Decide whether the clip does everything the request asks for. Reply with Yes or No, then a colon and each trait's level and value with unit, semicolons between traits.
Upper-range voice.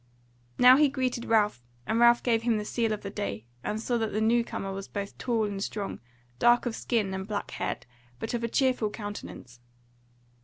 Yes: high, 220 Hz